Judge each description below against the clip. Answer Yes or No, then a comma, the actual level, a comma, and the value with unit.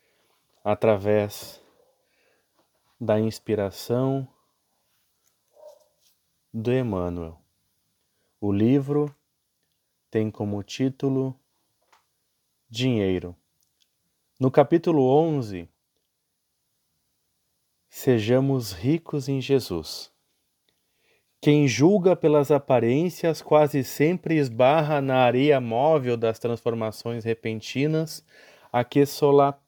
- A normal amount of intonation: Yes, average, 5.0 semitones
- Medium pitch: No, low, 130 Hz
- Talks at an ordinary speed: No, slow, 65 wpm